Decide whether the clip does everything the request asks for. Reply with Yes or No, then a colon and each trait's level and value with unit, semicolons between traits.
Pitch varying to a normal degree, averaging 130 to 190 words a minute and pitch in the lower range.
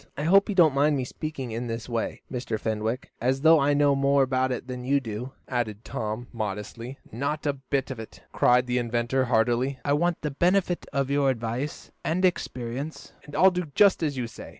No: average, 3.5 semitones; fast, 205 wpm; low, 130 Hz